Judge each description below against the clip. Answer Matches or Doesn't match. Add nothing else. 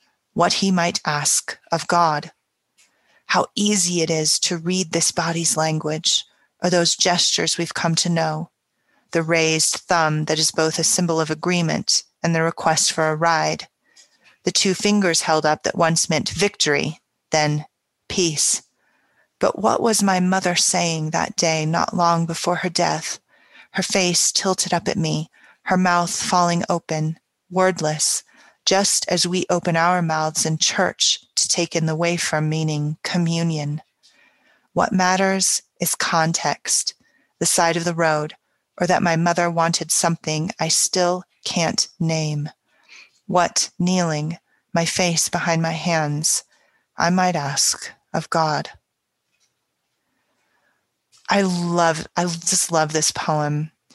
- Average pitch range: Doesn't match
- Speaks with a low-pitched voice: Doesn't match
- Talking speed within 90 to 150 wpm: Matches